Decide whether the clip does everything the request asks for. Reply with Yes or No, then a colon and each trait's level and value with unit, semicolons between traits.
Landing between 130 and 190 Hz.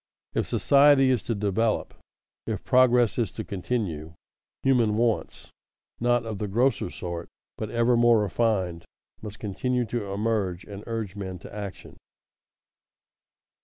No: low, 110 Hz